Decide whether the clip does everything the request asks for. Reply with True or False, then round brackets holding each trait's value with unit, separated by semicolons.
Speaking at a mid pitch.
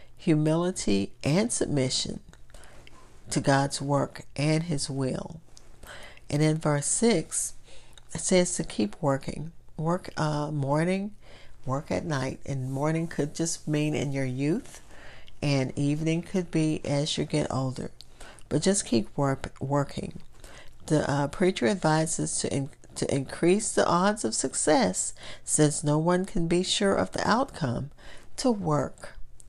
True (150 Hz)